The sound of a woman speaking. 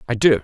No: male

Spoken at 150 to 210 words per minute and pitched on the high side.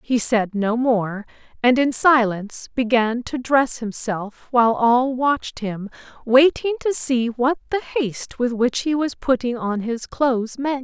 Yes: average, 165 wpm; high, 245 Hz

